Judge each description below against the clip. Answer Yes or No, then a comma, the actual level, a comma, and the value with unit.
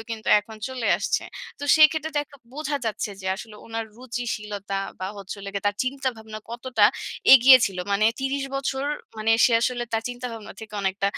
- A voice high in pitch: Yes, high, 225 Hz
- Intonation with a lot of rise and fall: No, average, 3.7 semitones